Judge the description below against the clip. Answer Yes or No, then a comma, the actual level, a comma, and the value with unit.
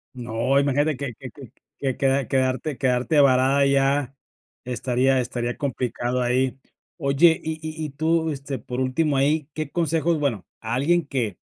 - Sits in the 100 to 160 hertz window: Yes, low, 135 Hz